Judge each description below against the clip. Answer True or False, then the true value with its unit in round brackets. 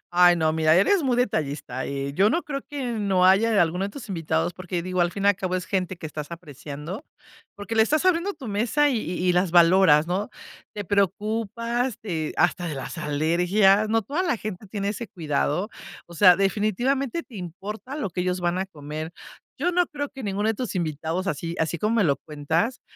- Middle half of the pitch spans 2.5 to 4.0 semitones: False (4.9 semitones)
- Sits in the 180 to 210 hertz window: True (190 Hz)